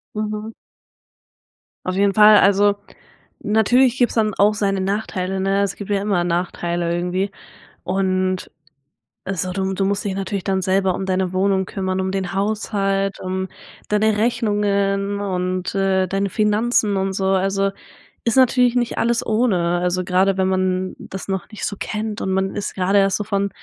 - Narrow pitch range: Yes, narrow, 1.7 semitones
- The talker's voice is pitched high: Yes, high, 195 Hz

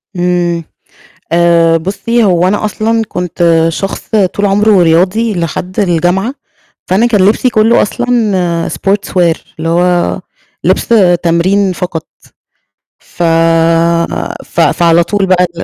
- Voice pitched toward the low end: No, medium, 180 Hz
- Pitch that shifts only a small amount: No, average, 3.3 semitones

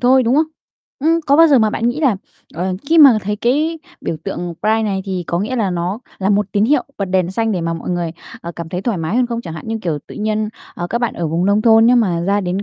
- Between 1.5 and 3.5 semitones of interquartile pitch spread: No, average, 5.1 semitones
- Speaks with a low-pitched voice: No, high, 210 Hz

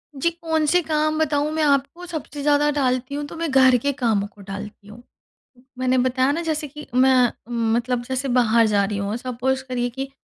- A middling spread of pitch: Yes, average, 3.6 semitones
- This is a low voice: No, very high, 265 Hz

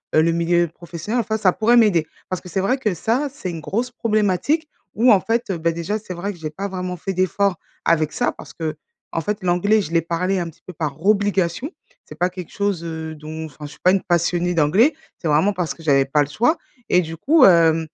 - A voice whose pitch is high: No, medium, 180 Hz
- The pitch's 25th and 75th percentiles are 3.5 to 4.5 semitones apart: Yes, average, 4.0 semitones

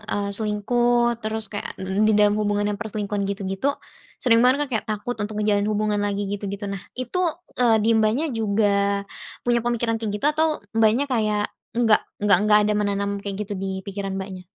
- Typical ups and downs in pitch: No, narrow, 2.0 semitones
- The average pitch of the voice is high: Yes, high, 210 Hz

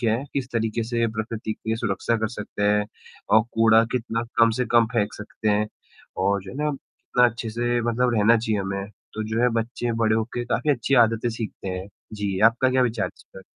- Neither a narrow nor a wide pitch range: No, narrow, 2.1 semitones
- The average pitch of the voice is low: Yes, low, 115 Hz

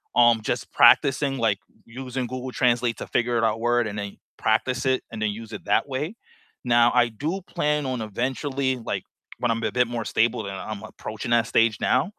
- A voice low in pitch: Yes, low, 120 Hz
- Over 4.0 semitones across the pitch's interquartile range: No, average, 2.7 semitones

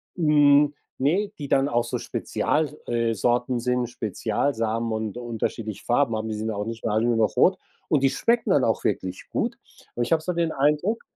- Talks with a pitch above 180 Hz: No, low, 120 Hz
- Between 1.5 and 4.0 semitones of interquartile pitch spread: No, average, 4.7 semitones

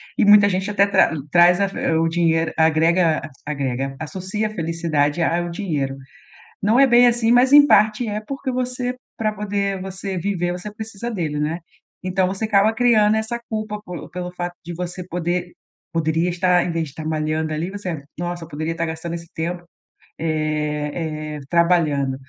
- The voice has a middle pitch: Yes, medium, 175 Hz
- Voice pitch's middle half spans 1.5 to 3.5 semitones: No, average, 4.3 semitones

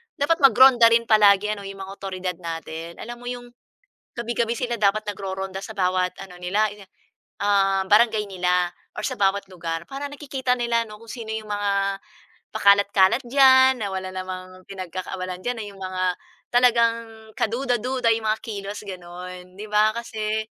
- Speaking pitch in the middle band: No, high, 205 Hz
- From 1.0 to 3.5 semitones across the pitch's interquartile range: No, average, 3.9 semitones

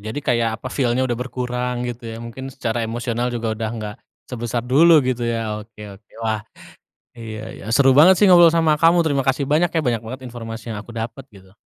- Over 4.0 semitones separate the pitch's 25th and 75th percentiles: No, average, 2.9 semitones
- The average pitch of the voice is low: Yes, low, 120 Hz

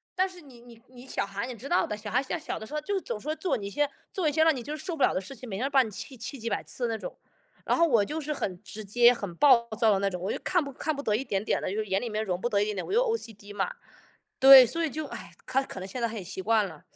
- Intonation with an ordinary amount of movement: No, wide, 5.9 semitones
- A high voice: Yes, high, 240 Hz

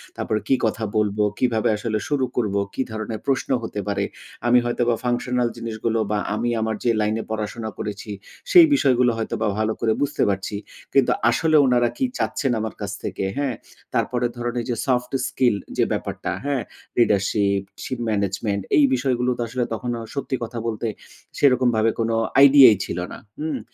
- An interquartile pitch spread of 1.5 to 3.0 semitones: Yes, narrow, 2.6 semitones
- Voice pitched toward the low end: Yes, low, 120 Hz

